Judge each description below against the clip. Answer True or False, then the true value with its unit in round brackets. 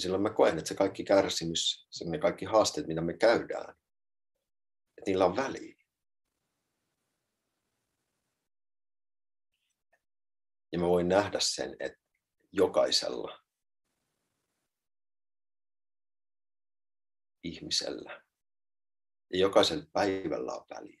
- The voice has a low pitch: True (100 Hz)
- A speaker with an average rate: False (90 wpm)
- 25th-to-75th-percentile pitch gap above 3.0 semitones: False (2.6 semitones)